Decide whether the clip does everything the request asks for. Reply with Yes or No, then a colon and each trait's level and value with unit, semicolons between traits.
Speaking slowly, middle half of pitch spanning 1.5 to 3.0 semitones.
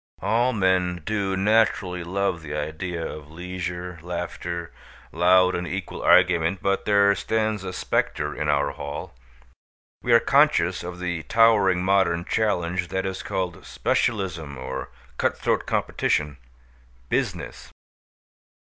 Yes: slow, 125 wpm; narrow, 2.5 semitones